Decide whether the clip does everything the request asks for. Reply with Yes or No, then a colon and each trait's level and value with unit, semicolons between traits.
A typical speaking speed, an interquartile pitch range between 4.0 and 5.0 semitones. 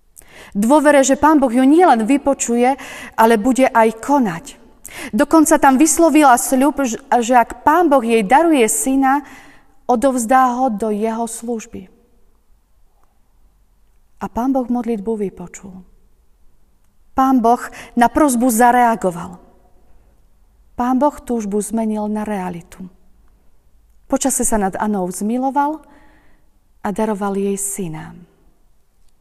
No: slow, 105 wpm; average, 4.6 semitones